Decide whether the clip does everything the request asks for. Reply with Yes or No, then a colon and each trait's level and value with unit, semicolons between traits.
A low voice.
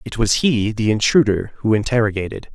Yes: low, 110 Hz